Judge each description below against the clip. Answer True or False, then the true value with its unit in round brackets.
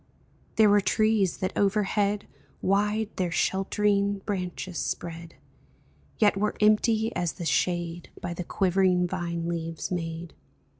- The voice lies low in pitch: False (190 Hz)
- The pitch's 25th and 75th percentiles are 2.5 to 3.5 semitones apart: True (3.2 semitones)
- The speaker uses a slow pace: True (120 wpm)